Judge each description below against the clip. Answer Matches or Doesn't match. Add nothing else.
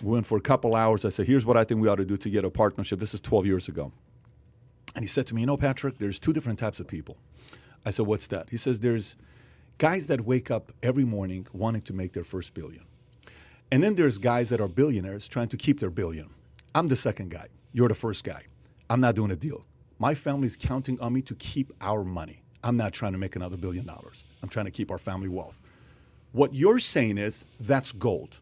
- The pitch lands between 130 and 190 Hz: Doesn't match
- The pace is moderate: Doesn't match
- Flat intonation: Doesn't match